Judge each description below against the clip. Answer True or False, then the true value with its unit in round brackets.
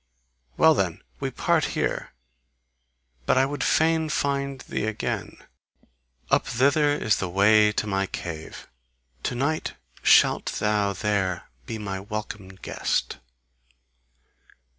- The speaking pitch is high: False (105 Hz)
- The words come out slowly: True (120 wpm)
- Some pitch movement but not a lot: False (6.1 semitones)